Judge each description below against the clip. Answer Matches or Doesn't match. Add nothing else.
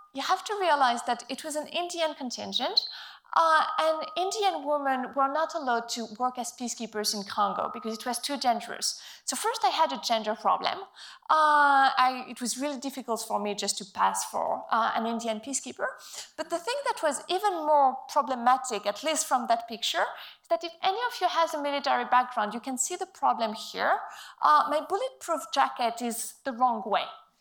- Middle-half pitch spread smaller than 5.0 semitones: Doesn't match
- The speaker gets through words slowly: Doesn't match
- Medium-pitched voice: Doesn't match